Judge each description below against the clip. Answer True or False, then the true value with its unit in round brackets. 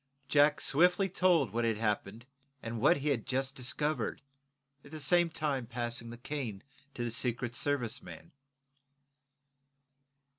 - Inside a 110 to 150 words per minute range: True (140 wpm)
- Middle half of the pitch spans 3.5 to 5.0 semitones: True (4.3 semitones)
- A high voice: False (130 Hz)